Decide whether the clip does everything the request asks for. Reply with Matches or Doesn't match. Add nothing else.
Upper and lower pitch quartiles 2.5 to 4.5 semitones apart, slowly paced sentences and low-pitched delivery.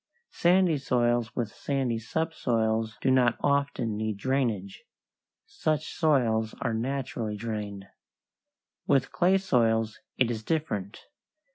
Matches